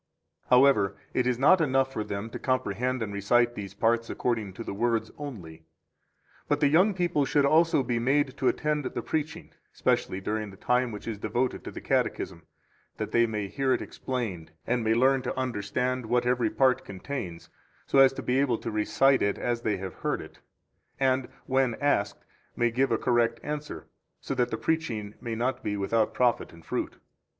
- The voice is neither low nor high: No, low, 120 Hz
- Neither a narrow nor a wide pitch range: Yes, average, 3.8 semitones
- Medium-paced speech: Yes, average, 195 wpm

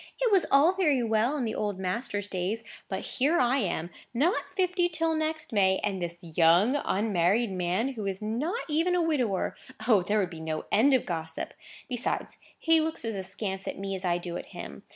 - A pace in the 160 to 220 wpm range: Yes, average, 200 wpm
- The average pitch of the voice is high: Yes, high, 220 Hz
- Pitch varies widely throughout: Yes, wide, 8.1 semitones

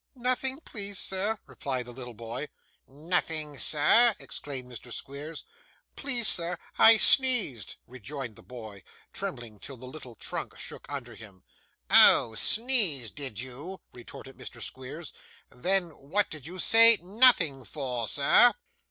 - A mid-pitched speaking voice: Yes, medium, 145 Hz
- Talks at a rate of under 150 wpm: Yes, slow, 135 wpm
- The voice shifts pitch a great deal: Yes, wide, 7.8 semitones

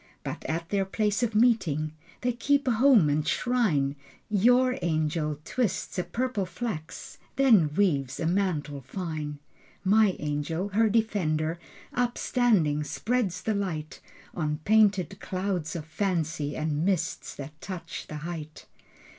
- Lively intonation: Yes, wide, 6.0 semitones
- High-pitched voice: No, medium, 180 Hz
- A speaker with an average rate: No, slow, 130 wpm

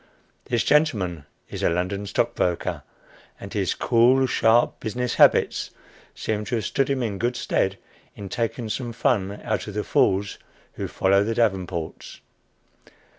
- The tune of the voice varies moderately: Yes, average, 3.6 semitones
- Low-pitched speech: Yes, low, 110 Hz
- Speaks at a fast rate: No, average, 145 wpm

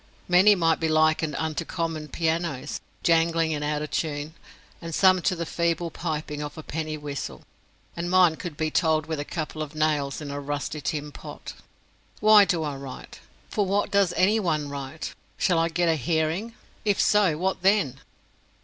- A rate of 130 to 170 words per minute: No, average, 180 wpm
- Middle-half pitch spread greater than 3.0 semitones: No, average, 2.7 semitones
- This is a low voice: No, medium, 160 Hz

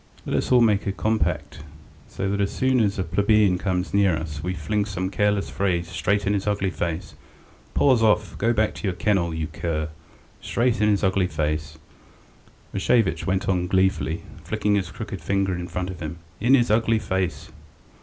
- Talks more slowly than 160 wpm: No, average, 185 wpm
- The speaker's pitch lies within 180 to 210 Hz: No, very low, 95 Hz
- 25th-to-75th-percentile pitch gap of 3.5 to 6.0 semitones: No, average, 3.1 semitones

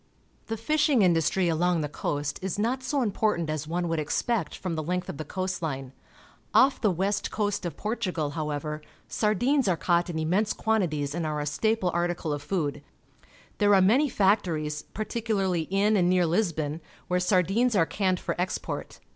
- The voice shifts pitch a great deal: No, average, 4.9 semitones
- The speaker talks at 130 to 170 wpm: No, average, 180 wpm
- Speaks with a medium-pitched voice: Yes, medium, 180 Hz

